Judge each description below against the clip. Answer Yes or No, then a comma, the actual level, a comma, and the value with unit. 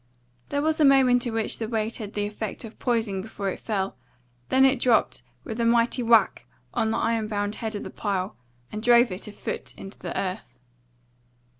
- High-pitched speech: Yes, high, 225 Hz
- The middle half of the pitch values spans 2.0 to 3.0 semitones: Yes, narrow, 2.6 semitones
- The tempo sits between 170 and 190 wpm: No, average, 200 wpm